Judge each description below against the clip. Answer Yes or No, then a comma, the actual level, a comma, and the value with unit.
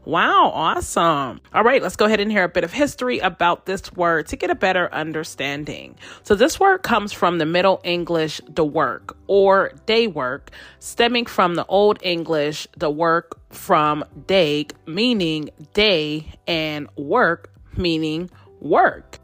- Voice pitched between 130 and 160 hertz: No, medium, 175 Hz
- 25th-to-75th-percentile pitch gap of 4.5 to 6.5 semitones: Yes, average, 4.8 semitones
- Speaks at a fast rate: No, average, 155 wpm